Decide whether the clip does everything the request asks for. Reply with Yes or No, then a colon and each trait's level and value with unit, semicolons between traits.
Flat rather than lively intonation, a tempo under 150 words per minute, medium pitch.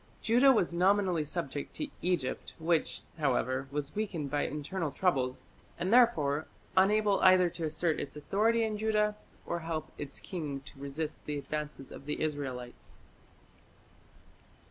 No: average, 5.2 semitones; average, 140 wpm; medium, 160 Hz